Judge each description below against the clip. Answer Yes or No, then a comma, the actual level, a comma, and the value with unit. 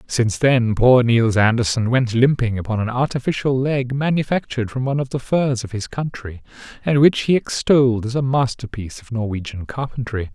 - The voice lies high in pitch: No, low, 120 Hz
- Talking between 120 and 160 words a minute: No, average, 175 wpm